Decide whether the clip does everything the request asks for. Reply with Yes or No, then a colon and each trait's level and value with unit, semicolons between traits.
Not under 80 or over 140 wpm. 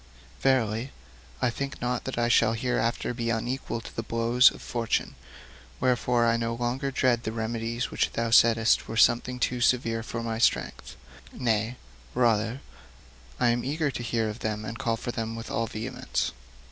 No: average, 170 wpm